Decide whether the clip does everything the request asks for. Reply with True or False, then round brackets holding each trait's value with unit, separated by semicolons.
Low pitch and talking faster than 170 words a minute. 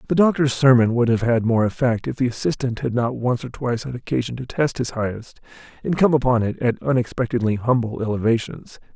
True (125 Hz; 200 wpm)